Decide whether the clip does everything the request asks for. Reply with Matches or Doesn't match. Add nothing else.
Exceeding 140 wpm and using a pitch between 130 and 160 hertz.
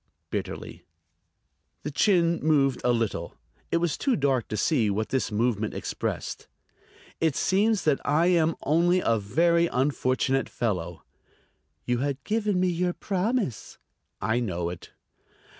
Doesn't match